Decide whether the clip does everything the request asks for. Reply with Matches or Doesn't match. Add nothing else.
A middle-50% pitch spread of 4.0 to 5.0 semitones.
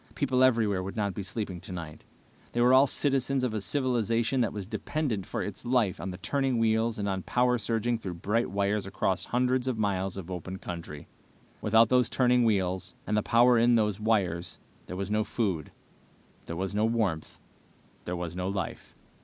Matches